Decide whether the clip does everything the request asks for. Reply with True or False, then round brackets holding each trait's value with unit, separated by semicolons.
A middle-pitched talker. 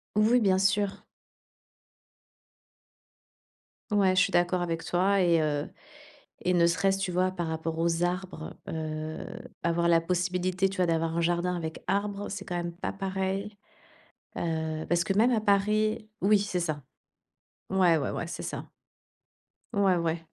True (180 Hz)